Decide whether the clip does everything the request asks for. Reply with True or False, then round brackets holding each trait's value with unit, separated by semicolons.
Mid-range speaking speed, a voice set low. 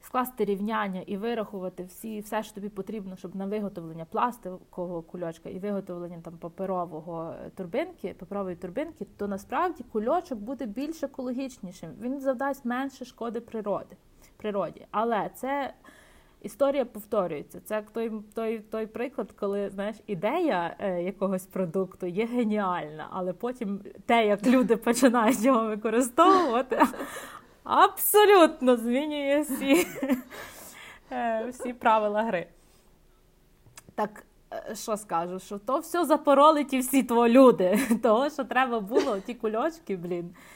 False (120 wpm; 220 Hz)